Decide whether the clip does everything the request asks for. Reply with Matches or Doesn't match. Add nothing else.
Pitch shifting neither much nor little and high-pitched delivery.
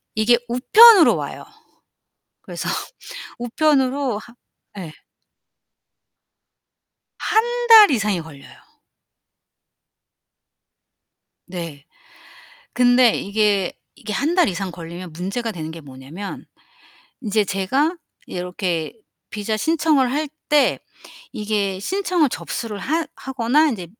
Doesn't match